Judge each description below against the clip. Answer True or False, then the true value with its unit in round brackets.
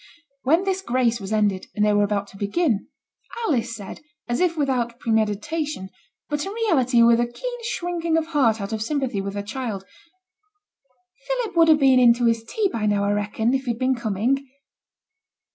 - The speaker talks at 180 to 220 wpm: True (185 wpm)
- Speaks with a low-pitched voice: False (240 Hz)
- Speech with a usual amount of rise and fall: False (6.5 semitones)